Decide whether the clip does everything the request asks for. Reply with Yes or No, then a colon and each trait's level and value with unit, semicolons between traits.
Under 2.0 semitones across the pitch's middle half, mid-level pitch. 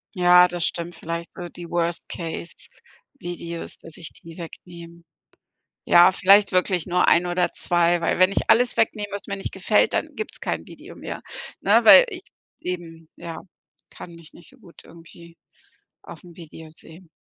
Yes: narrow, 1.5 semitones; medium, 175 Hz